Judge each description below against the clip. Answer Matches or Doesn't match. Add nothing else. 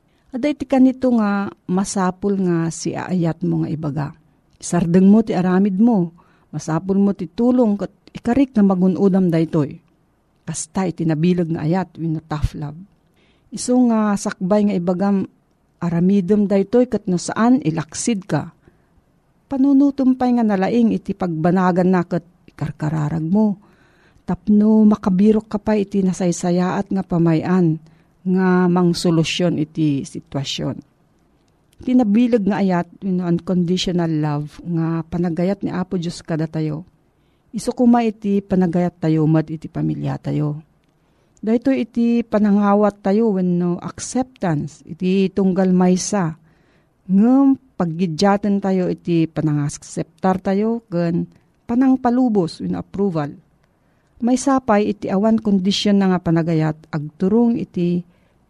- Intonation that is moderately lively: Matches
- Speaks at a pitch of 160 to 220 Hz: Matches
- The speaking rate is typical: Matches